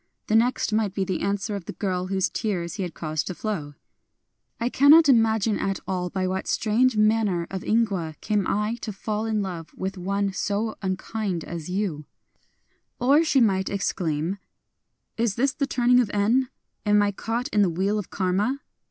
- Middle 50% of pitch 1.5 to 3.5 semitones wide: Yes, average, 3.1 semitones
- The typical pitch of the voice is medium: No, high, 205 Hz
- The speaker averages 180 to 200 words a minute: Yes, average, 190 wpm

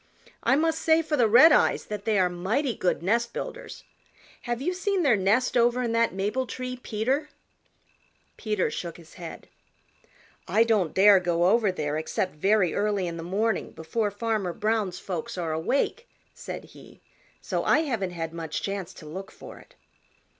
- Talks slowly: No, average, 170 wpm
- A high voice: Yes, high, 210 Hz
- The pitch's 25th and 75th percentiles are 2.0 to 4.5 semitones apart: No, average, 5.2 semitones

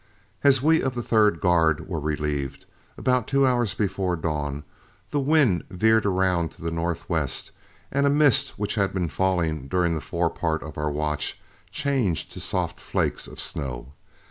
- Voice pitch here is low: Yes, very low, 90 Hz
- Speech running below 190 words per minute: Yes, average, 170 wpm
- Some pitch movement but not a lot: No, wide, 7.4 semitones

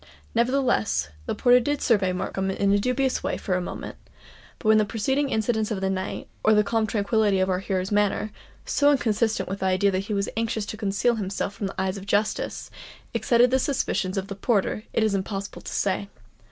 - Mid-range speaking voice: No, high, 205 Hz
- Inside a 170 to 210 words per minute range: Yes, average, 200 wpm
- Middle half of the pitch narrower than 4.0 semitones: Yes, average, 3.0 semitones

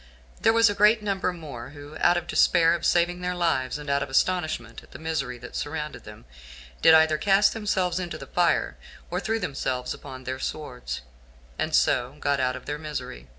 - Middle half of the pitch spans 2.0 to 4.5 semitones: No, wide, 5.5 semitones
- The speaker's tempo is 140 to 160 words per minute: No, average, 195 wpm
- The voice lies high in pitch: No, medium, 155 Hz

